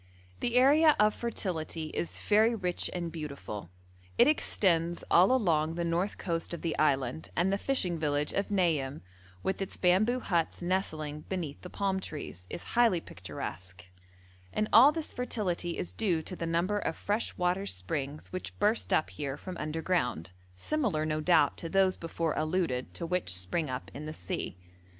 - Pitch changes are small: No, average, 4.3 semitones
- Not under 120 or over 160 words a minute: No, average, 170 wpm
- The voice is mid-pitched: Yes, medium, 170 Hz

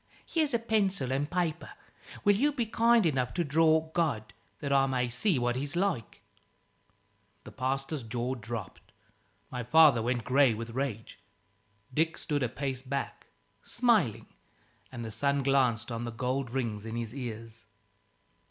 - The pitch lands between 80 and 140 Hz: Yes, low, 135 Hz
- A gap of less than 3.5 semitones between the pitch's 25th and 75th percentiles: No, average, 5.2 semitones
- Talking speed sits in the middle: Yes, average, 150 wpm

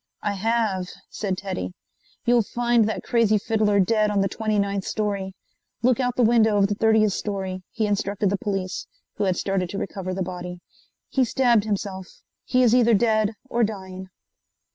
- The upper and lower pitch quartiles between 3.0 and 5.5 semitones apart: No, narrow, 2.6 semitones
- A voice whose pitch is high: Yes, high, 205 Hz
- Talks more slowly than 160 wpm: No, average, 175 wpm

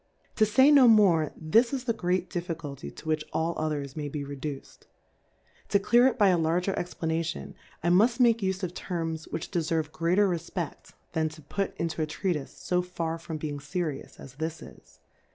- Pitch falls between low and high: Yes, medium, 165 Hz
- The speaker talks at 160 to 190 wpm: Yes, average, 180 wpm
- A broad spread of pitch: No, average, 3.7 semitones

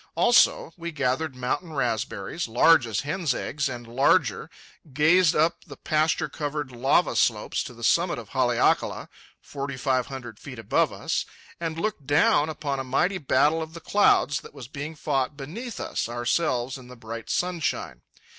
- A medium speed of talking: Yes, average, 165 wpm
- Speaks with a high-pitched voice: No, medium, 140 Hz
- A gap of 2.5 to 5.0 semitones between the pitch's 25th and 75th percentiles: Yes, average, 4.1 semitones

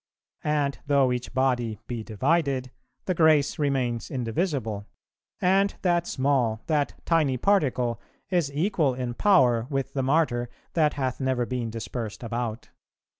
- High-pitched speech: No, low, 130 Hz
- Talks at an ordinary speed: No, slow, 130 wpm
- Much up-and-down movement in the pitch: No, average, 4.0 semitones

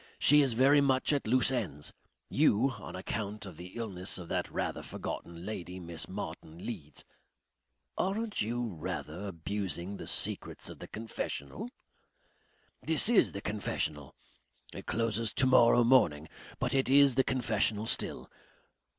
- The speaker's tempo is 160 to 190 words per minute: No, average, 145 wpm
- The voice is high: No, low, 110 Hz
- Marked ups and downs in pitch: Yes, wide, 6.5 semitones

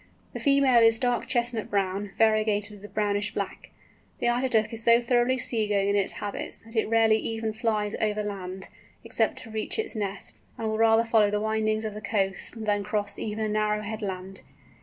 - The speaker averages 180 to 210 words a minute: Yes, average, 200 wpm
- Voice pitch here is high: Yes, high, 215 Hz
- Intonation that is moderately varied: No, narrow, 1.7 semitones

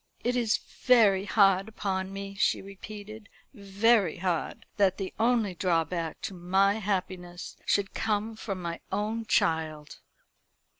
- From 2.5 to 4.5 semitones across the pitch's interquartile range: Yes, average, 2.8 semitones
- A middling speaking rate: No, slow, 130 wpm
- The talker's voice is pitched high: Yes, high, 195 Hz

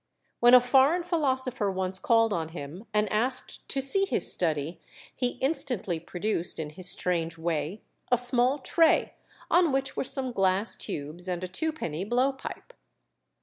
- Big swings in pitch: Yes, wide, 7.1 semitones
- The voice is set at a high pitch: Yes, high, 220 Hz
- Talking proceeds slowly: No, average, 155 wpm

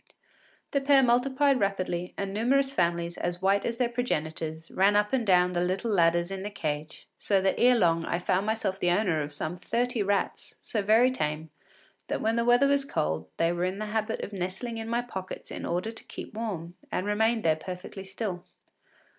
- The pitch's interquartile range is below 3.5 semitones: No, average, 4.8 semitones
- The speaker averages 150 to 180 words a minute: No, average, 200 wpm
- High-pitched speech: Yes, high, 195 Hz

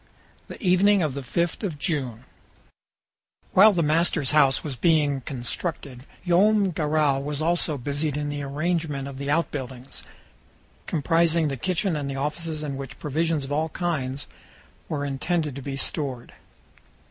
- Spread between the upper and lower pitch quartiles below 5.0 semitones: Yes, average, 3.3 semitones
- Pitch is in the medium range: Yes, medium, 150 Hz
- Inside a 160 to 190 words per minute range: No, average, 145 wpm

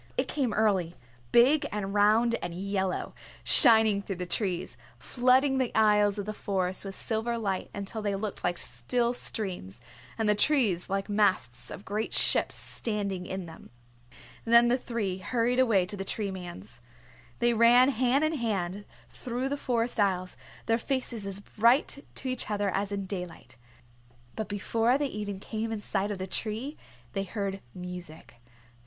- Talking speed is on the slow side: No, average, 165 wpm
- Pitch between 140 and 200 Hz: No, high, 210 Hz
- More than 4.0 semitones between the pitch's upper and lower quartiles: No, average, 3.5 semitones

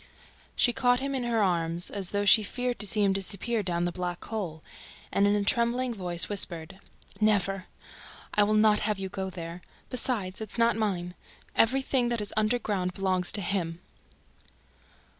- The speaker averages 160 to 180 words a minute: Yes, average, 170 wpm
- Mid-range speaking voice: No, high, 205 Hz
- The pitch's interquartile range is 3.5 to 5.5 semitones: Yes, average, 3.8 semitones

